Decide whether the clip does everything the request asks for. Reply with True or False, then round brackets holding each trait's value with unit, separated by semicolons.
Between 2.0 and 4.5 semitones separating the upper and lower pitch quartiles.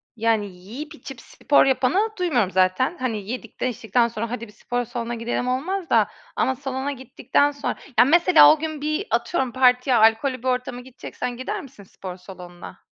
True (3.7 semitones)